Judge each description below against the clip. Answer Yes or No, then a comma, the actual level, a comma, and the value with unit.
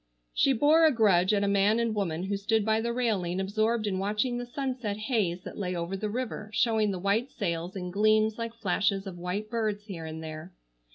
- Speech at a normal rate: No, fast, 215 wpm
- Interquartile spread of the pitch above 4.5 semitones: No, average, 3.2 semitones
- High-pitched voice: Yes, high, 210 Hz